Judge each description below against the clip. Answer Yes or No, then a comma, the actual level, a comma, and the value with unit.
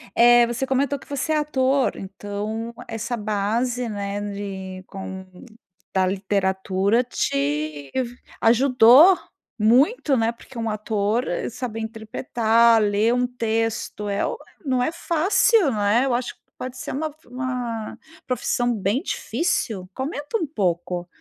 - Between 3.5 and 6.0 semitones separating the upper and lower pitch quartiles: Yes, average, 4.2 semitones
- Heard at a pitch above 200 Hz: Yes, high, 225 Hz